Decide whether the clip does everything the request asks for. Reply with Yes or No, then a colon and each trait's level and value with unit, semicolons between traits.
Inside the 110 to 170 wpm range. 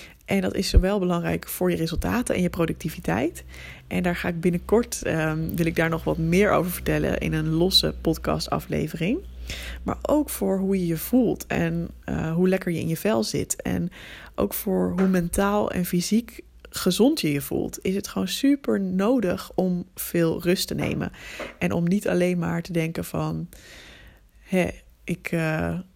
No: average, 180 wpm